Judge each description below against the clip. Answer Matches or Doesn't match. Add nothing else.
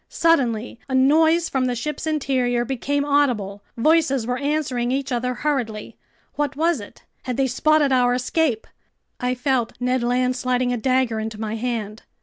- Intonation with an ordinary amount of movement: Matches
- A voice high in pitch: Matches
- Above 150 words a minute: Matches